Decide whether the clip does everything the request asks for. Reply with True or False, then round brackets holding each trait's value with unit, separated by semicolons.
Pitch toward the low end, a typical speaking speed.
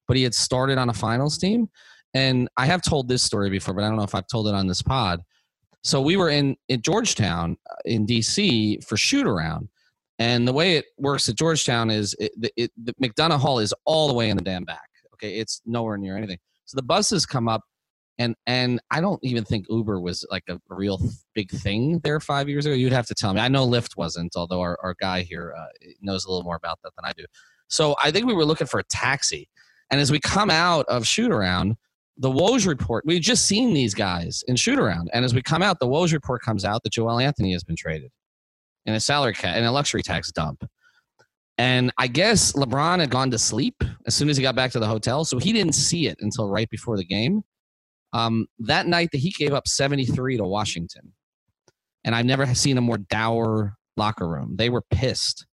False (120 Hz; 230 wpm)